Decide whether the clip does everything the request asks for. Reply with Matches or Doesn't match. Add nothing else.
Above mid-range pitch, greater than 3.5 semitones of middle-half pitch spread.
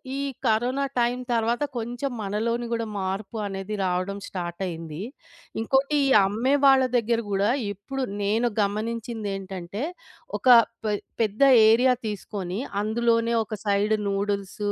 Doesn't match